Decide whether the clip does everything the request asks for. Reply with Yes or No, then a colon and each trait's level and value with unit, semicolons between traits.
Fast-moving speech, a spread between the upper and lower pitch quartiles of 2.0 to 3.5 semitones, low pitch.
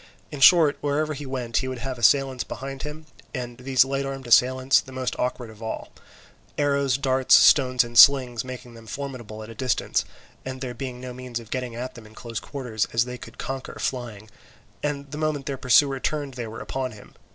Yes: fast, 210 wpm; narrow, 2.4 semitones; low, 130 Hz